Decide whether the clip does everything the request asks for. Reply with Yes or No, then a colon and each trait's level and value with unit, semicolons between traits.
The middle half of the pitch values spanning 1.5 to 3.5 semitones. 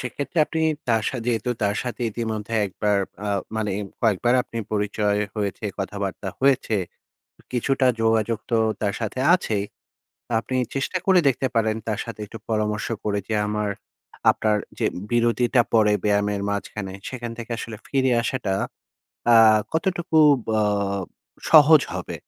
Yes: average, 3.2 semitones